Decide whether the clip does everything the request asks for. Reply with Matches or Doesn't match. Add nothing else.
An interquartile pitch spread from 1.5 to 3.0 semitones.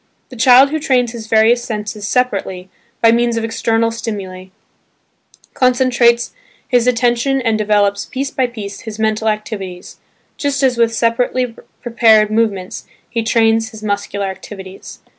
Matches